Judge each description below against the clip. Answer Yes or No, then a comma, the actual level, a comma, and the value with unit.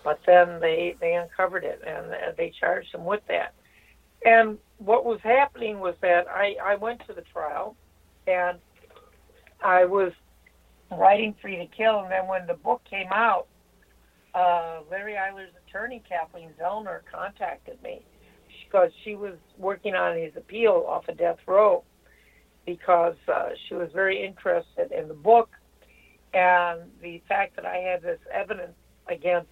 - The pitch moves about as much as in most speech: Yes, average, 4.6 semitones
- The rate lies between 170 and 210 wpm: No, average, 155 wpm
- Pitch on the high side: Yes, high, 195 Hz